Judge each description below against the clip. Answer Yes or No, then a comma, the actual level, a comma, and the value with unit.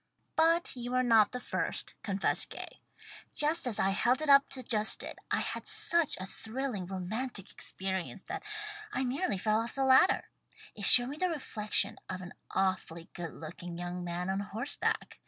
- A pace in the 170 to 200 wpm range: Yes, average, 180 wpm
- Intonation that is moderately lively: No, wide, 6.0 semitones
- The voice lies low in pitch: No, high, 220 Hz